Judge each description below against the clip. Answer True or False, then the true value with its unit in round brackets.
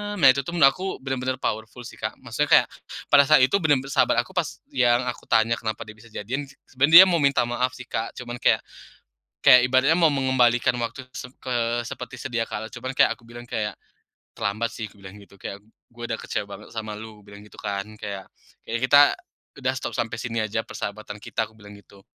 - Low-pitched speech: True (120 Hz)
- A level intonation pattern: False (3.1 semitones)